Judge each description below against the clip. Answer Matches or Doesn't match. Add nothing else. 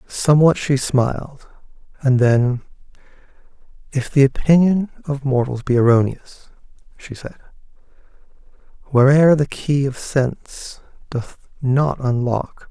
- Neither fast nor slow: Doesn't match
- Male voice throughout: Matches